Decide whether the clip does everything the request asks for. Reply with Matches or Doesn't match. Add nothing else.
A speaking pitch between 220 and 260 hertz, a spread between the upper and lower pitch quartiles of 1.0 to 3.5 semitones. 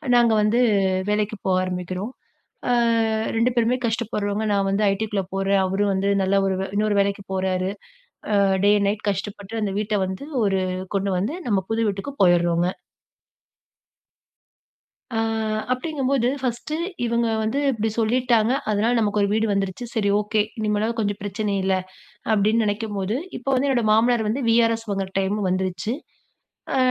Doesn't match